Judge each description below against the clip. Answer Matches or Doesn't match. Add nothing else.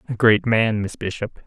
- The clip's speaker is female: Doesn't match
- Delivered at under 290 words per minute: Matches